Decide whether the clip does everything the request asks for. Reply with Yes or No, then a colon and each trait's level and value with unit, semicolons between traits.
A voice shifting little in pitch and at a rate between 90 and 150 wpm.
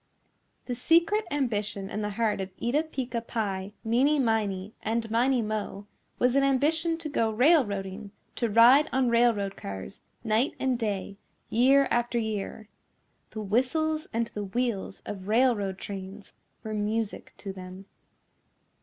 No: average, 4.2 semitones; average, 140 wpm